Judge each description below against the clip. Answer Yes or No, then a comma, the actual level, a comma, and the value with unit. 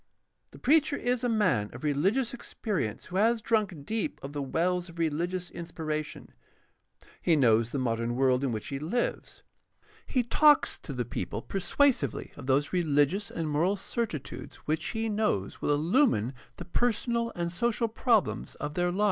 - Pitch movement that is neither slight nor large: No, wide, 7.9 semitones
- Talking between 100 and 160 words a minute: No, average, 170 wpm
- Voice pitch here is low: No, medium, 175 Hz